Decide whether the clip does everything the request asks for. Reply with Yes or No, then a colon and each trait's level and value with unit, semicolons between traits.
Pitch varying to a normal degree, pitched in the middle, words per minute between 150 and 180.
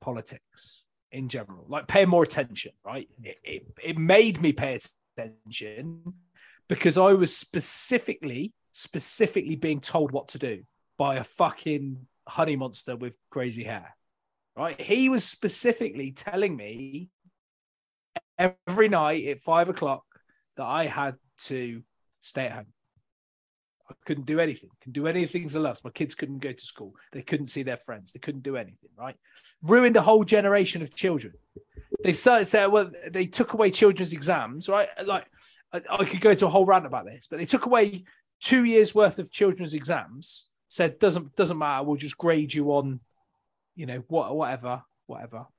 No: wide, 6.2 semitones; medium, 165 Hz; average, 165 wpm